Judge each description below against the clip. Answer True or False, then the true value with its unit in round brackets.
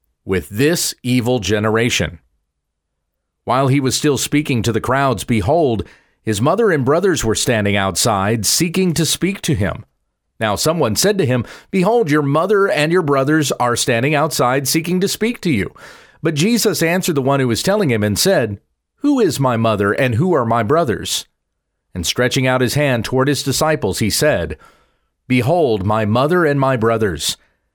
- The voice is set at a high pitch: False (130 Hz)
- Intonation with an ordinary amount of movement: False (6.5 semitones)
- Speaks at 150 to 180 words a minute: True (175 wpm)